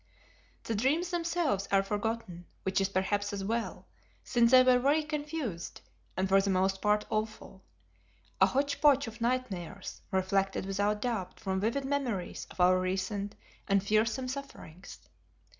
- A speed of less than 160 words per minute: Yes, average, 145 wpm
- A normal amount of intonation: Yes, average, 4.9 semitones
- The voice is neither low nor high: No, high, 210 Hz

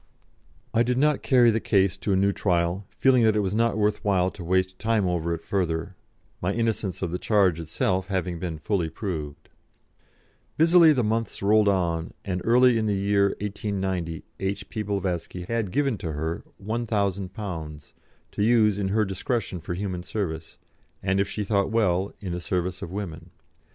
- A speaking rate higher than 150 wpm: Yes, average, 170 wpm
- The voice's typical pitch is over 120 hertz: No, low, 100 Hz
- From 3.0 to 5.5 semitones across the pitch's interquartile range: Yes, average, 3.4 semitones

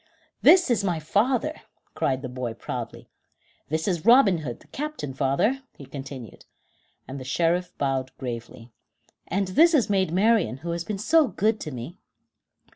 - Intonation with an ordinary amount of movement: No, wide, 8.3 semitones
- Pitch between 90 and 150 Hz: No, medium, 170 Hz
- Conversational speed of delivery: Yes, average, 160 wpm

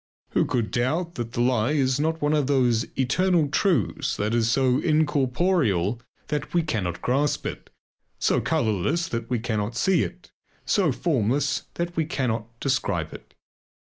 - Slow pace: No, average, 155 wpm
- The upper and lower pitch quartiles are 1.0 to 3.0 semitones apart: No, average, 5.0 semitones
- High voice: No, low, 130 Hz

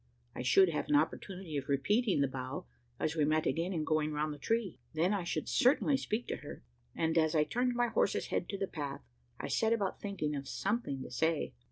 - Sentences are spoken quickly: Yes, fast, 220 wpm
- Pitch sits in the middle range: Yes, medium, 165 Hz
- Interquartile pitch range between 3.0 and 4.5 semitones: No, wide, 5.6 semitones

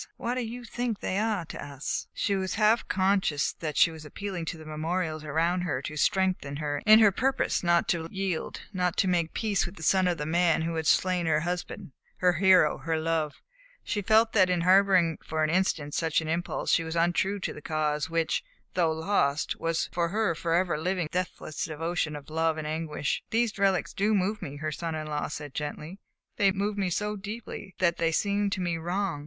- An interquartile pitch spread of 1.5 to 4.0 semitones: Yes, average, 3.5 semitones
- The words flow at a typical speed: No, fast, 215 wpm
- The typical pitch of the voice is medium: Yes, medium, 175 Hz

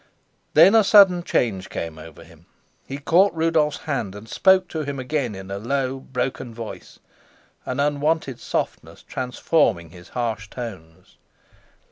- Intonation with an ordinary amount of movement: No, wide, 6.9 semitones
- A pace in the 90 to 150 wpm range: Yes, average, 140 wpm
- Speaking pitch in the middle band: No, low, 130 Hz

